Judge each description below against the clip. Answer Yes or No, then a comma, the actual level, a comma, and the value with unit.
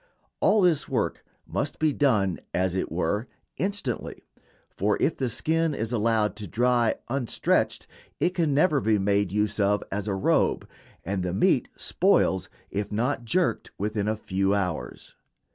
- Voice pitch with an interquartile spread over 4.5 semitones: Yes, wide, 5.6 semitones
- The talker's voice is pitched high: No, low, 110 Hz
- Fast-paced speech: No, average, 155 wpm